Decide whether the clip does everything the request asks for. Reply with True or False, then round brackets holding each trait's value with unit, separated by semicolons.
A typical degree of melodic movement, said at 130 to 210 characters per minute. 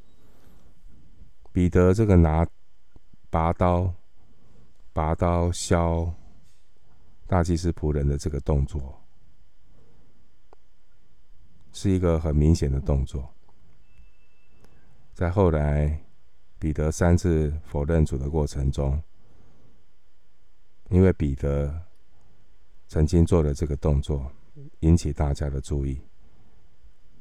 True (3.4 semitones; 135 characters per minute)